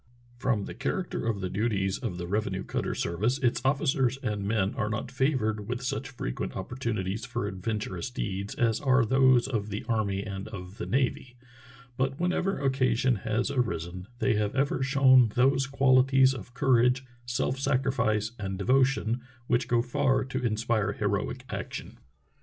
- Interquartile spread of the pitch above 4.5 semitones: No, average, 4.1 semitones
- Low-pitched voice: Yes, low, 120 Hz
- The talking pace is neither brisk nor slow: Yes, average, 160 wpm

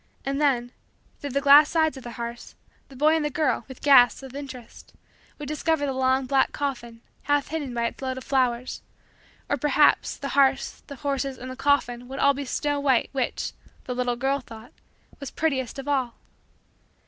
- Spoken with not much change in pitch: Yes, narrow, 2.3 semitones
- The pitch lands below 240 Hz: No, very high, 270 Hz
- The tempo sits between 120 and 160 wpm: No, average, 190 wpm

